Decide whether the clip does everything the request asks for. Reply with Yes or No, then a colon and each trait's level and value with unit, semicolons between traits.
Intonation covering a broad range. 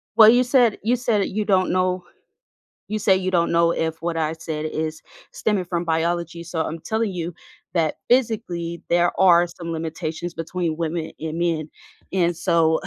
No: narrow, 2.5 semitones